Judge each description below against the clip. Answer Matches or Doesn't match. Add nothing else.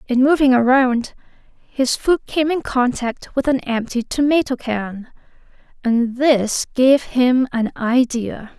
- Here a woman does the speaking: Matches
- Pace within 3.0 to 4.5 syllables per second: Matches